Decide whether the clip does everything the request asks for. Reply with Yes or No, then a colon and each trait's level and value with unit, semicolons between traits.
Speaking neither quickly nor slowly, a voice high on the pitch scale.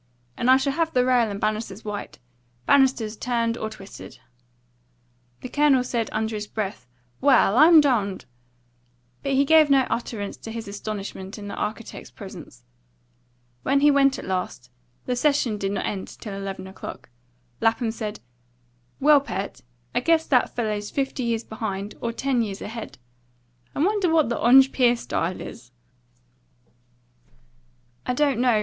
Yes: average, 150 wpm; high, 230 Hz